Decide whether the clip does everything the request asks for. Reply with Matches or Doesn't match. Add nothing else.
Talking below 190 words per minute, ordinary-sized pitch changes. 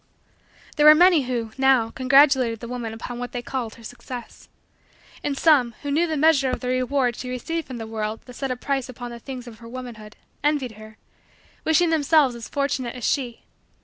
Doesn't match